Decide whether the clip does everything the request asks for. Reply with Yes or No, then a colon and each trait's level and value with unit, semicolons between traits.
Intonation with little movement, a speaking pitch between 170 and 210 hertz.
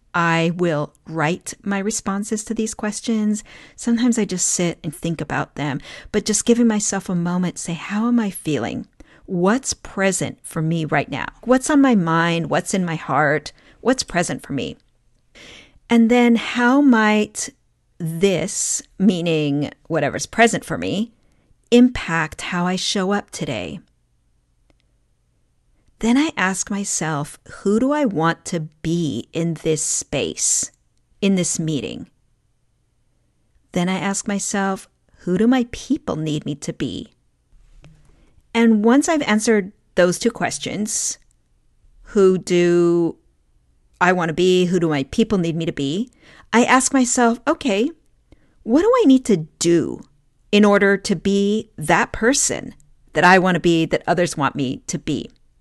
No: wide, 5.4 semitones; medium, 185 Hz